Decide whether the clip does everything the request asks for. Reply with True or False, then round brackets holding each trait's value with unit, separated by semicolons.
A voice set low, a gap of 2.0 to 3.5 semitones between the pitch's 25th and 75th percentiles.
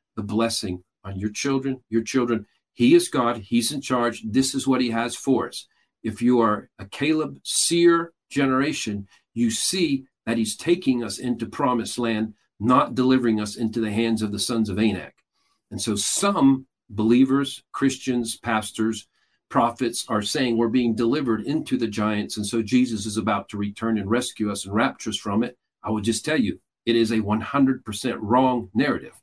True (115 Hz; 3.2 semitones)